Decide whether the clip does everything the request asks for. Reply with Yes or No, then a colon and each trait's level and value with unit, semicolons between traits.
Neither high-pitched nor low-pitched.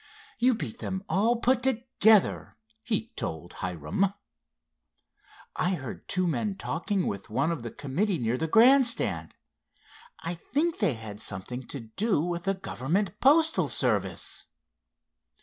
Yes: medium, 175 Hz